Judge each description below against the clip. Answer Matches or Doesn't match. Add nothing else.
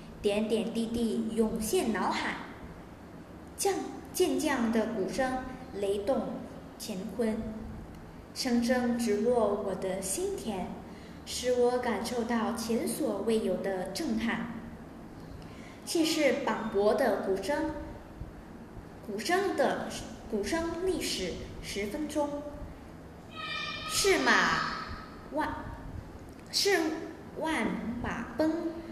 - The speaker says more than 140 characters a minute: Doesn't match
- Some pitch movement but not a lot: Doesn't match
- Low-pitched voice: Doesn't match